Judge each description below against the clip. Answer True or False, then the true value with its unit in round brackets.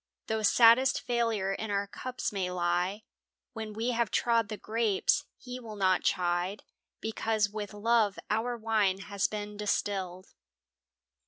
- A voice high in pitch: True (210 Hz)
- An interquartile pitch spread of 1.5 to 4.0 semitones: True (2.7 semitones)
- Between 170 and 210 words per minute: False (140 wpm)